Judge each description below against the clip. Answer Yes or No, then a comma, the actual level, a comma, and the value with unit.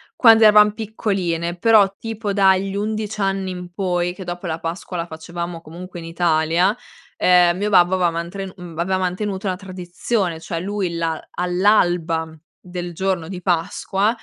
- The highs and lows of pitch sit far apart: No, narrow, 2.4 semitones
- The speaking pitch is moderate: Yes, medium, 180 Hz